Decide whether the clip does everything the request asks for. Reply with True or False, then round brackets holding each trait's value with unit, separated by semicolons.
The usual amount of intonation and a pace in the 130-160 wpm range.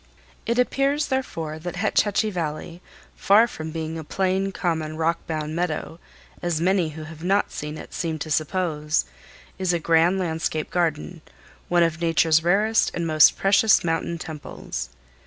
True (3.1 semitones; 155 wpm)